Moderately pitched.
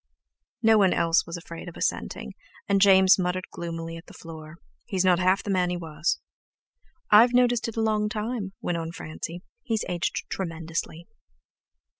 Yes: medium, 180 Hz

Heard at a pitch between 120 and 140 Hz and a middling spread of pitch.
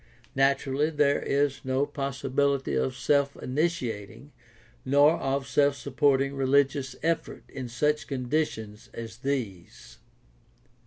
No: low, 135 Hz; narrow, 2.0 semitones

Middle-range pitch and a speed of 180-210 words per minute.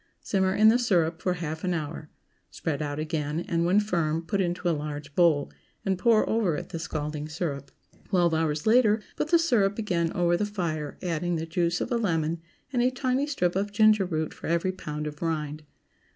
Yes: medium, 170 Hz; average, 200 wpm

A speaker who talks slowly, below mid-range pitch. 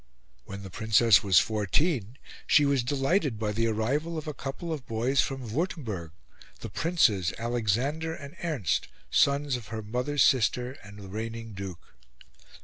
No: average, 150 wpm; low, 120 Hz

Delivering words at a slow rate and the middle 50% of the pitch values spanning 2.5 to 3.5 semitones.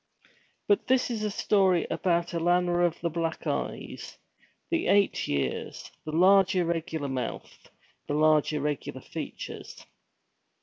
Yes: slow, 120 wpm; average, 3.2 semitones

